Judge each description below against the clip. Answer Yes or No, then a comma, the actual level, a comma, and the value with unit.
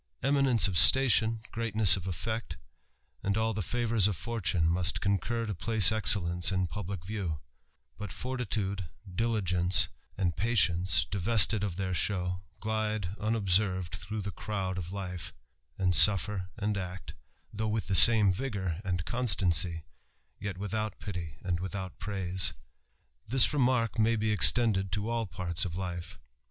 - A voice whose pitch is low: Yes, low, 100 Hz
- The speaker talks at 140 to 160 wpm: Yes, average, 145 wpm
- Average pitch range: Yes, average, 3.4 semitones